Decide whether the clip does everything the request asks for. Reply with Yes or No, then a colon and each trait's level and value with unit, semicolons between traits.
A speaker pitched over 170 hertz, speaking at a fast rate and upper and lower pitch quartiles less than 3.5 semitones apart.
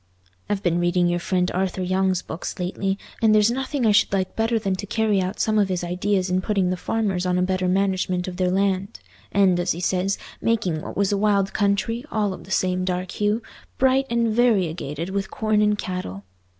Yes: high, 190 Hz; fast, 210 wpm; narrow, 2.5 semitones